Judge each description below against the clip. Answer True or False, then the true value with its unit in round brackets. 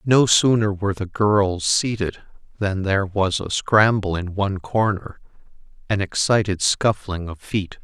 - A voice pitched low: True (100 Hz)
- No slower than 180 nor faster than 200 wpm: False (145 wpm)